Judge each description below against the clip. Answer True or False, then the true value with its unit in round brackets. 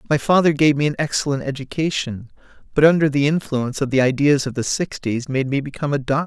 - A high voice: False (140 Hz)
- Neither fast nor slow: False (210 wpm)